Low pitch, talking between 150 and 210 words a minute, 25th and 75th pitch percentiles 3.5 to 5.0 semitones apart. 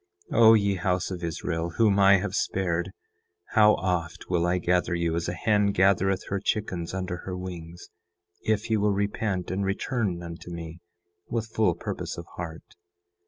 No: very low, 95 Hz; average, 170 wpm; average, 2.8 semitones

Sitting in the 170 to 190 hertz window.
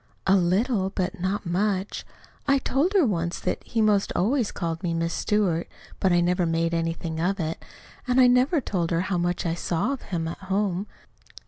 Yes: medium, 185 Hz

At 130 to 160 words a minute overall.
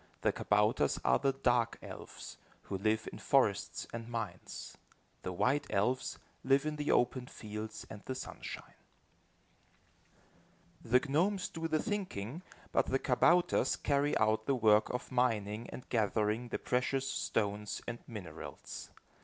Yes: slow, 135 wpm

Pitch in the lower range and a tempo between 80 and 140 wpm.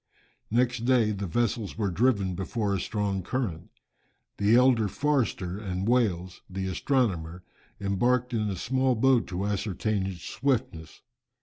Yes: low, 105 Hz; slow, 135 wpm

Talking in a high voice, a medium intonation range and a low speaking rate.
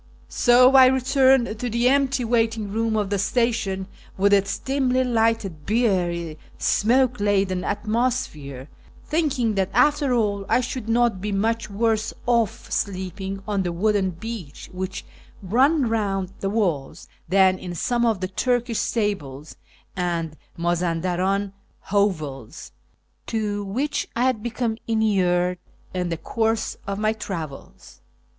Yes: high, 210 Hz; average, 4.2 semitones; slow, 130 wpm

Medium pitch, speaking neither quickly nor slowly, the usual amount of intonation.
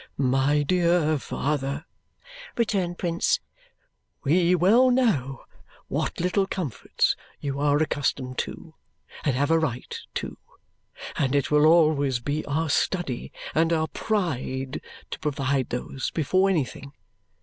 No: medium, 150 Hz; slow, 120 wpm; average, 4.2 semitones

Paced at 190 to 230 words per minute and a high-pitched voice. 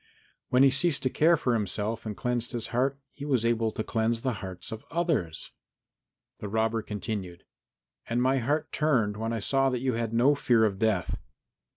No: average, 195 wpm; low, 115 Hz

